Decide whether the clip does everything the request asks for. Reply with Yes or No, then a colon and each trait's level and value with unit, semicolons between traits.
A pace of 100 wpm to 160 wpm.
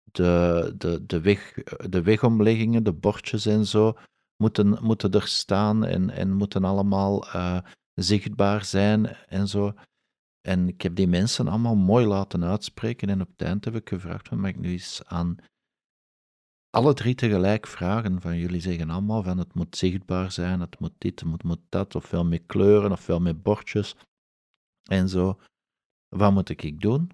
No: average, 170 wpm